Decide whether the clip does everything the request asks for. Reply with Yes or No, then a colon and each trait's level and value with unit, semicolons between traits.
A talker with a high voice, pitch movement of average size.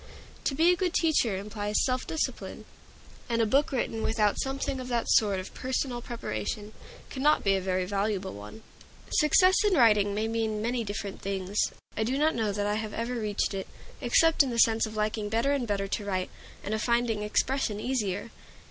Yes: high, 220 Hz; average, 3.8 semitones